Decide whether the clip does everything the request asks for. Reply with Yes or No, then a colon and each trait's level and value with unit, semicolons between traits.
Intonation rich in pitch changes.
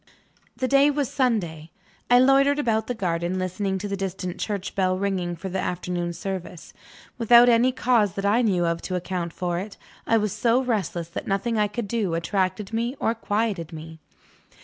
No: average, 4.4 semitones